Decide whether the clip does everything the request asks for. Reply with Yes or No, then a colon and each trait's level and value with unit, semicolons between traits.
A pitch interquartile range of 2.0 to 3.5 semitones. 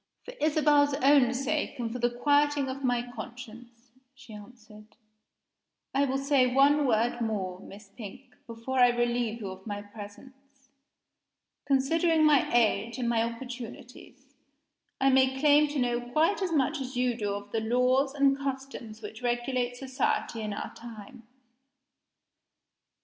Yes: average, 3.0 semitones